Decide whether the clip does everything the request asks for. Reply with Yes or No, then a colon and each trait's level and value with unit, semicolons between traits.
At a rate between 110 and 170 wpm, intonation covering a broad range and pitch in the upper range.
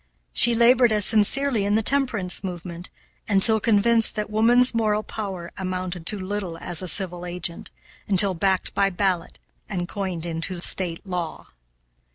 No: average, 150 wpm; average, 3.5 semitones; high, 195 Hz